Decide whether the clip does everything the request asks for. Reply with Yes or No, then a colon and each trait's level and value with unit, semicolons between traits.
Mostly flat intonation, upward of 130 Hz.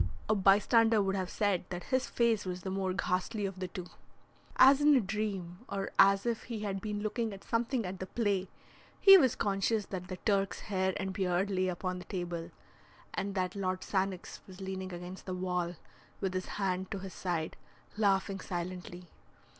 Yes: narrow, 2.2 semitones; high, 190 Hz